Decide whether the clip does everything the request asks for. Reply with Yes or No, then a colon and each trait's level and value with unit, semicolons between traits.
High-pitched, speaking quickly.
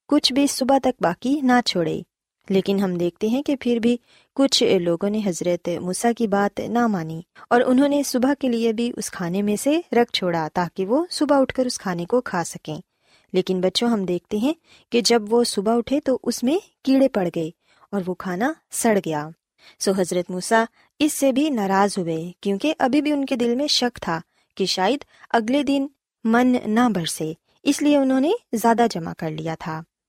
Yes: high, 230 Hz; fast, 200 wpm